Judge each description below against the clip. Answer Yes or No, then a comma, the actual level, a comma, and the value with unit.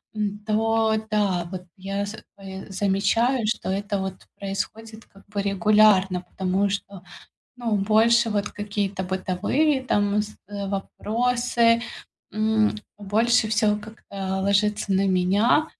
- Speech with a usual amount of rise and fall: No, narrow, 2.1 semitones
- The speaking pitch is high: Yes, high, 205 Hz